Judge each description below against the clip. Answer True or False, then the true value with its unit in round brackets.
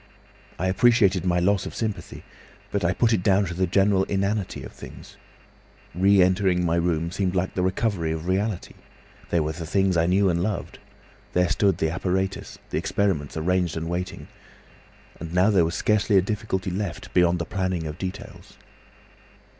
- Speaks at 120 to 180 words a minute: True (175 wpm)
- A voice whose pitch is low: True (95 Hz)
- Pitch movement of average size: False (2.3 semitones)